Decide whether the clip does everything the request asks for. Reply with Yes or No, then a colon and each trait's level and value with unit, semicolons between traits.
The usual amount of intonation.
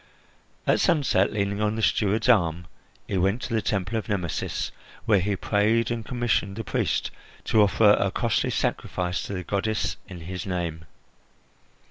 Yes: average, 3.0 semitones